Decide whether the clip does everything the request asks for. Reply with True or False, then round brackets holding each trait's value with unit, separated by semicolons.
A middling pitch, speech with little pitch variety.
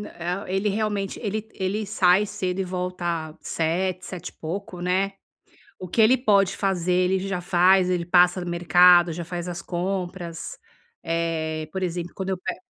True (180 Hz; 1.9 semitones)